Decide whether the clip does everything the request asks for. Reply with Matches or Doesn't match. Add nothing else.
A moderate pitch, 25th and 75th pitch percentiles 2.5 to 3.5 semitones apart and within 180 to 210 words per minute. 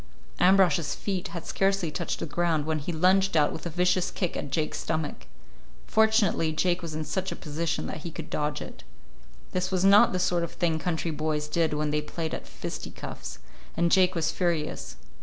Matches